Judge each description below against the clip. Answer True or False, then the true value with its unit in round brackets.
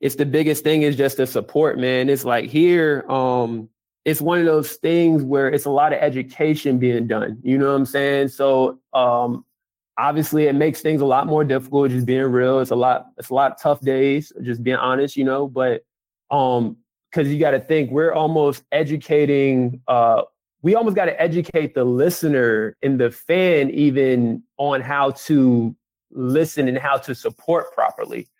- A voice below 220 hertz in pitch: True (140 Hz)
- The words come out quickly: False (185 wpm)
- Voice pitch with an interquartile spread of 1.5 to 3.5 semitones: True (3.0 semitones)